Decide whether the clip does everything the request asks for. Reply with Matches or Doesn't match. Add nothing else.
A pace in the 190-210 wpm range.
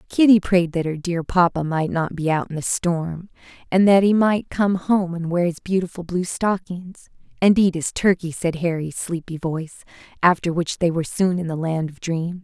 Matches